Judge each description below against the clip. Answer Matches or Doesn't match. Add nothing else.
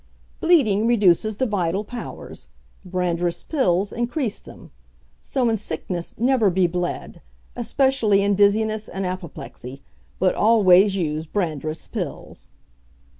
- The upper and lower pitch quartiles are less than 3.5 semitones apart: Doesn't match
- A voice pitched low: Doesn't match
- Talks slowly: Matches